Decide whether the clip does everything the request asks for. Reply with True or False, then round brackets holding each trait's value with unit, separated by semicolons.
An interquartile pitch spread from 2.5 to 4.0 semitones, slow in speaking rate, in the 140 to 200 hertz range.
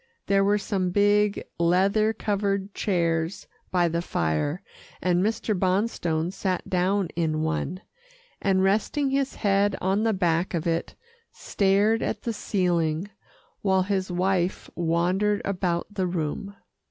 True (2.8 semitones; 130 wpm; 190 Hz)